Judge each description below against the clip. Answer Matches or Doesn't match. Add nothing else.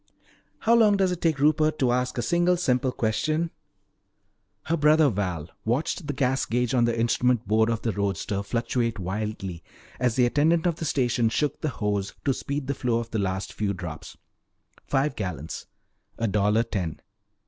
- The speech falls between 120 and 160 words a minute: Doesn't match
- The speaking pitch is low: Matches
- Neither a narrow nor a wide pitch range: Doesn't match